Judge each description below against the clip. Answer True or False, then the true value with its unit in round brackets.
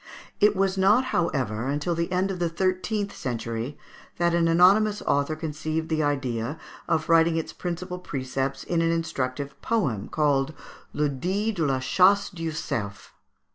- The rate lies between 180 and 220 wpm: False (155 wpm)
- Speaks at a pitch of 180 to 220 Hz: False (165 Hz)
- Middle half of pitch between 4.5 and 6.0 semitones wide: True (4.9 semitones)